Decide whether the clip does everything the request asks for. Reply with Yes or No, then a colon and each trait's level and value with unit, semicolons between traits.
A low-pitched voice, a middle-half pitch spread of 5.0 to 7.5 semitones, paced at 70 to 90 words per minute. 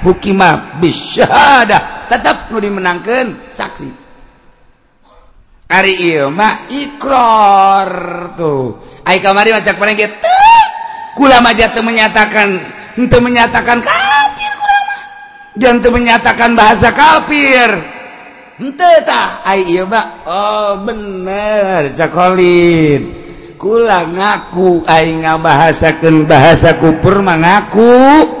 No: high, 215 Hz; wide, 5.5 semitones; slow, 85 wpm